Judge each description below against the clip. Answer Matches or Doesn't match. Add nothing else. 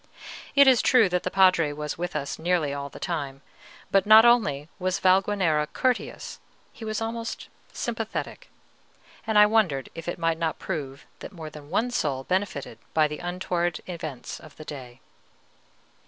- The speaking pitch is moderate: Matches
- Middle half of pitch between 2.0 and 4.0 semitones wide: Doesn't match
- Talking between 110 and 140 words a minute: Doesn't match